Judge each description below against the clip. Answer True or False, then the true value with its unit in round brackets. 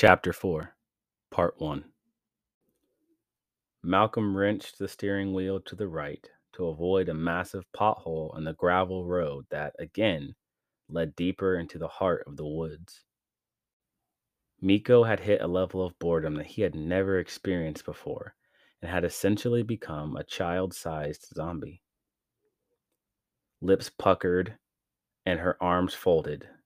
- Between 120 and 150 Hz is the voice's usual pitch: False (95 Hz)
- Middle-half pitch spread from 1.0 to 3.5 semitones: True (2.7 semitones)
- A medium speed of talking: False (130 wpm)